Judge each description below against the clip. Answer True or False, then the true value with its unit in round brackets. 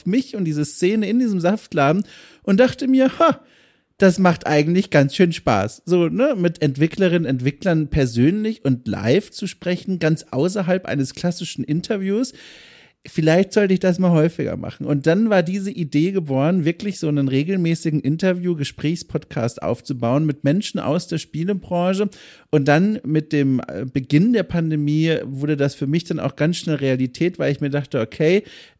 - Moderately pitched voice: True (165 Hz)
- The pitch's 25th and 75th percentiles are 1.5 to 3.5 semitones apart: False (4.6 semitones)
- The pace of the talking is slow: False (160 wpm)